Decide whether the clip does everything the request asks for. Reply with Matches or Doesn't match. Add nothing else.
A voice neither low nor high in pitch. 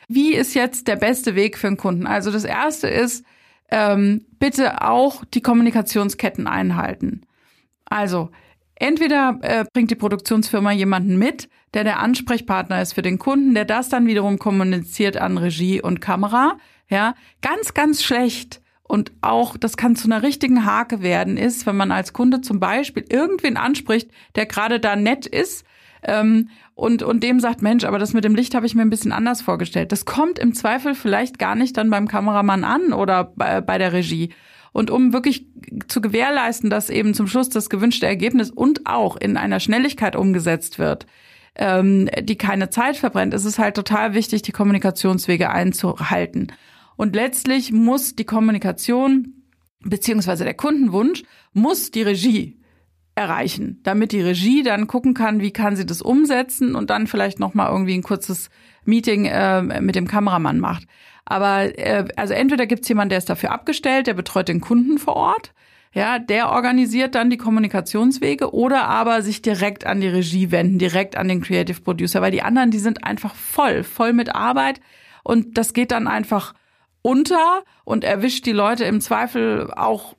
Doesn't match